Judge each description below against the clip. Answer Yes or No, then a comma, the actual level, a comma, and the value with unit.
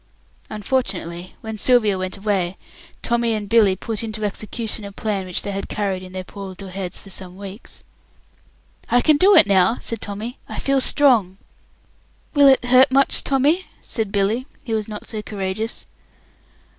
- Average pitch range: Yes, average, 3.6 semitones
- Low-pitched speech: No, high, 210 Hz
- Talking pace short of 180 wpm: Yes, average, 170 wpm